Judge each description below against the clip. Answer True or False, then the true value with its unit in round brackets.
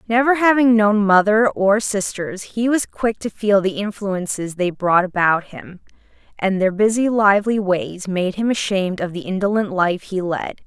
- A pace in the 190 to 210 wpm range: False (175 wpm)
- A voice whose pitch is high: True (200 Hz)